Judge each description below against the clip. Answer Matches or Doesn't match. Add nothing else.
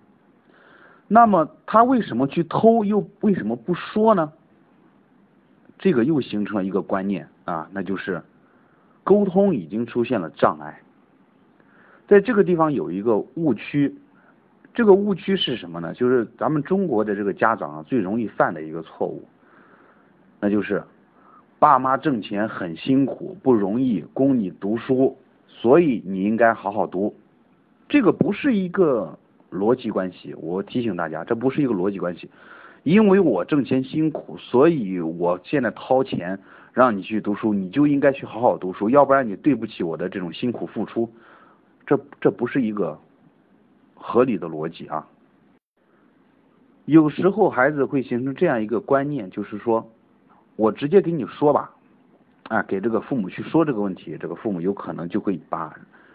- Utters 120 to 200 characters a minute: Doesn't match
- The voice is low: Matches